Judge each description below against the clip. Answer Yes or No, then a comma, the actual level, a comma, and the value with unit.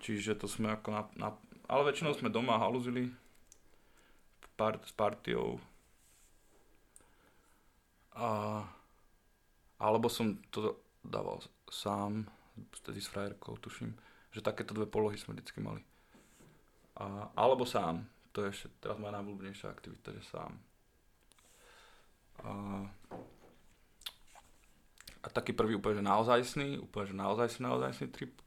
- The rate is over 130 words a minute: No, average, 115 wpm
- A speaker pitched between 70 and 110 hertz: Yes, low, 105 Hz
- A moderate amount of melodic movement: No, narrow, 1.6 semitones